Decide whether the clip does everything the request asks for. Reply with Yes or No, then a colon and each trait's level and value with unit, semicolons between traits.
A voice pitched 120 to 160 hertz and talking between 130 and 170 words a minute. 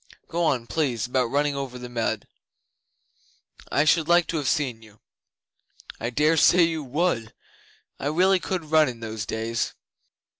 Yes: medium, 140 Hz; average, 160 wpm